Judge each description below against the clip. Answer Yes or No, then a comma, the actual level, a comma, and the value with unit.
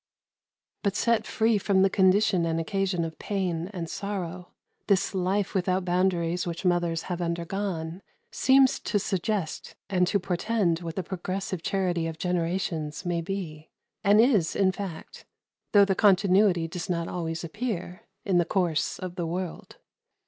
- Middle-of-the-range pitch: Yes, medium, 180 Hz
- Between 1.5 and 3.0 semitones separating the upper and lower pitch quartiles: Yes, average, 2.7 semitones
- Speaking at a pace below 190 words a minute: Yes, average, 150 wpm